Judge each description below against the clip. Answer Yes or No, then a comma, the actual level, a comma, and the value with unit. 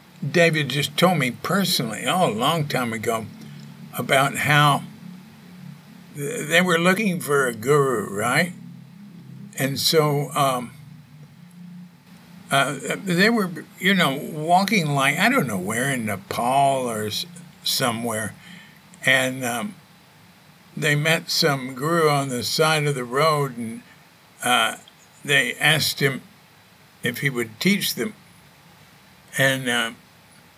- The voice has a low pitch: No, medium, 165 Hz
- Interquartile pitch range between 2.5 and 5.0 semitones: Yes, average, 4.4 semitones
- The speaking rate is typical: No, slow, 120 wpm